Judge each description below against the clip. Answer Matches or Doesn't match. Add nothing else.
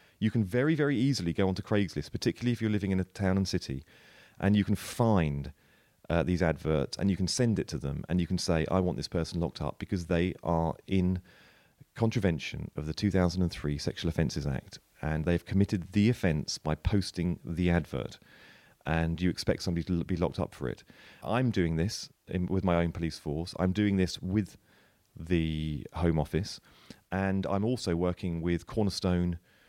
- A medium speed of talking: Matches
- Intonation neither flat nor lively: Matches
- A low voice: Matches